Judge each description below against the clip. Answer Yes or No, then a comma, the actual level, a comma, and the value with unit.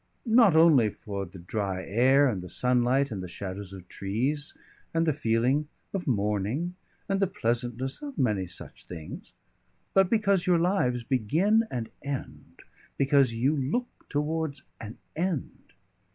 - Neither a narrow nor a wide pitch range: No, wide, 7.3 semitones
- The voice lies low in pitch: Yes, low, 130 Hz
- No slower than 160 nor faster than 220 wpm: No, average, 145 wpm